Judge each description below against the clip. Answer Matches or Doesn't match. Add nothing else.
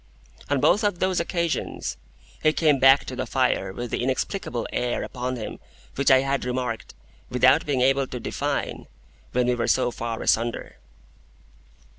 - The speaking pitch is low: Matches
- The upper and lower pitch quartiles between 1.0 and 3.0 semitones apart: Matches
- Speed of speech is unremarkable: Matches